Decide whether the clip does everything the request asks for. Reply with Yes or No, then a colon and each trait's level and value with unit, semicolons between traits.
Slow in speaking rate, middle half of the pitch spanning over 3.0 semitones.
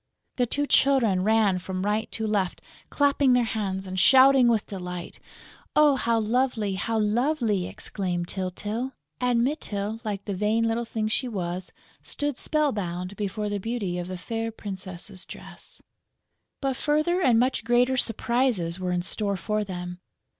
No: average, 155 wpm; average, 4.7 semitones